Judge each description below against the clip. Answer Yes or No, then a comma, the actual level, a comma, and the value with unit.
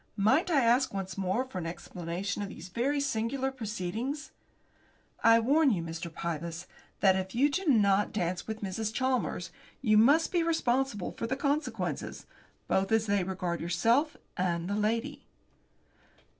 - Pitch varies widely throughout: Yes, wide, 6.3 semitones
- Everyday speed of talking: Yes, average, 155 wpm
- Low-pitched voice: No, high, 215 Hz